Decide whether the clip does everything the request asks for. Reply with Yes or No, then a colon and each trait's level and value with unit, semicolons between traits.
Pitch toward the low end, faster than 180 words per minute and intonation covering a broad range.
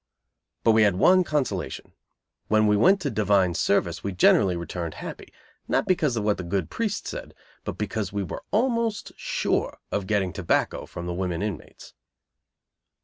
No: low, 105 Hz; average, 165 wpm; wide, 6.4 semitones